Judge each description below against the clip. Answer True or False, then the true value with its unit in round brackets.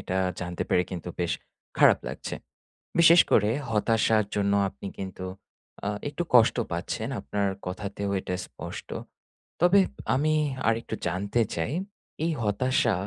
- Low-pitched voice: True (105 Hz)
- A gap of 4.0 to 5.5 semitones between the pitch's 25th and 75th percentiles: True (4.3 semitones)